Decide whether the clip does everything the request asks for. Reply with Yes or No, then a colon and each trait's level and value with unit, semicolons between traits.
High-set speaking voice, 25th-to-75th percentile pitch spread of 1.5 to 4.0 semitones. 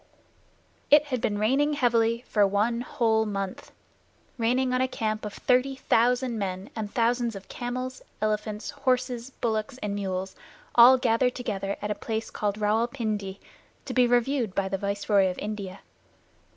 Yes: high, 225 Hz; average, 3.4 semitones